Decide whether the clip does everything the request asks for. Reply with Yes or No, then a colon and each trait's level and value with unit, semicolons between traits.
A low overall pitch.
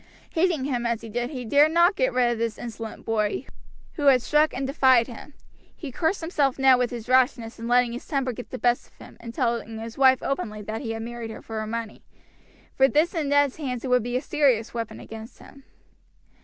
No: very high, 250 Hz